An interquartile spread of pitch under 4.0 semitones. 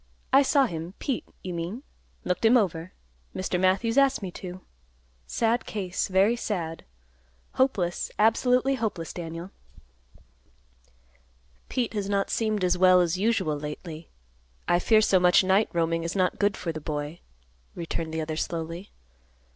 No: average, 4.6 semitones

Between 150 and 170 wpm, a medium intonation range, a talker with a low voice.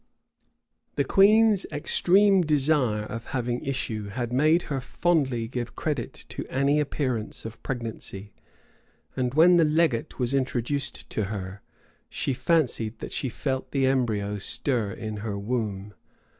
No: slow, 135 wpm; average, 5.0 semitones; low, 130 Hz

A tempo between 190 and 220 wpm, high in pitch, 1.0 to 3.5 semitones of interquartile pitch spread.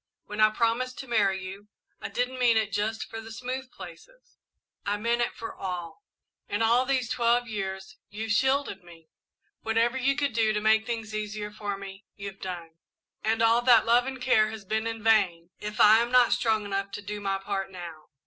Yes: average, 200 wpm; high, 220 Hz; average, 3.0 semitones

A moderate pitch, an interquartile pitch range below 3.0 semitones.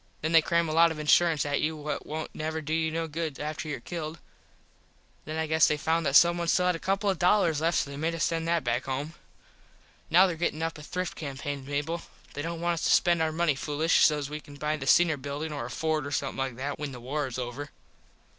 Yes: medium, 155 Hz; narrow, 2.5 semitones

